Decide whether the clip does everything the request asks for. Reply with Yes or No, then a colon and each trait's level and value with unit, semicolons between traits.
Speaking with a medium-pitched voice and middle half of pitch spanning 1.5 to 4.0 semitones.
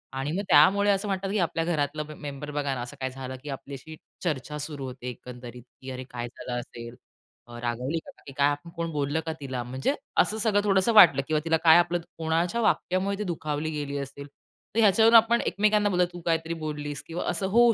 No: medium, 150 Hz; average, 5.0 semitones